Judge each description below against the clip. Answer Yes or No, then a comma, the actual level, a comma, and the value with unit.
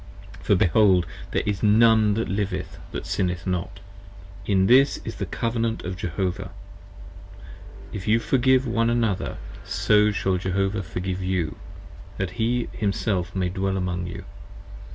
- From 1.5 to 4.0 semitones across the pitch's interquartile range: Yes, average, 3.4 semitones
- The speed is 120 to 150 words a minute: Yes, average, 140 wpm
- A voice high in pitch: No, low, 100 Hz